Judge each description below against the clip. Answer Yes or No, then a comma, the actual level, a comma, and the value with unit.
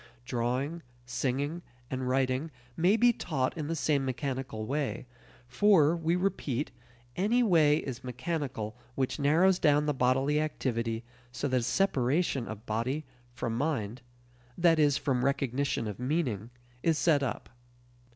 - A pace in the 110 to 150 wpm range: Yes, average, 140 wpm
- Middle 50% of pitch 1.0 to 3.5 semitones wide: No, average, 4.2 semitones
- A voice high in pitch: No, medium, 140 Hz